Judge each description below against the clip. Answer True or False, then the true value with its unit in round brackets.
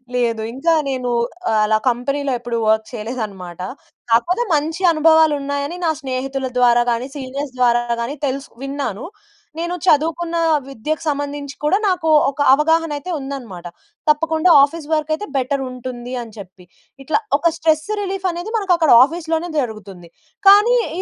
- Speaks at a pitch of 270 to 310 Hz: True (280 Hz)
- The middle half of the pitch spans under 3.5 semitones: False (4.8 semitones)